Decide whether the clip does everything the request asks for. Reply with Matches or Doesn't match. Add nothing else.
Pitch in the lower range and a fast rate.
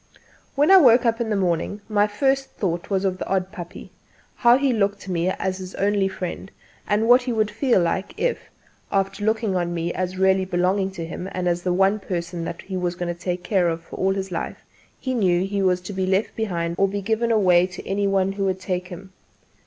Doesn't match